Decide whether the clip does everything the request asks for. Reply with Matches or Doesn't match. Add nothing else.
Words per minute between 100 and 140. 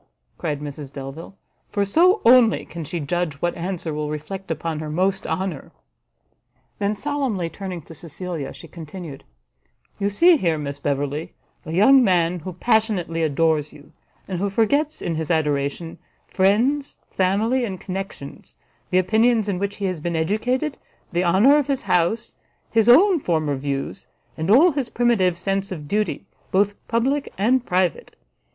Doesn't match